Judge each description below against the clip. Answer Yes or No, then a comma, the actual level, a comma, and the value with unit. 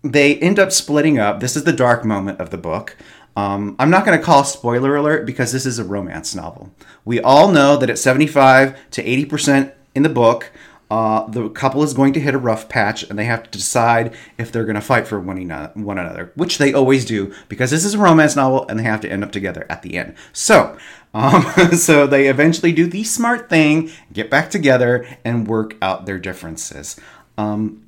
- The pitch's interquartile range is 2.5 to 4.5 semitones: No, wide, 5.5 semitones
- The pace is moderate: No, fast, 215 wpm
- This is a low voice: Yes, low, 130 Hz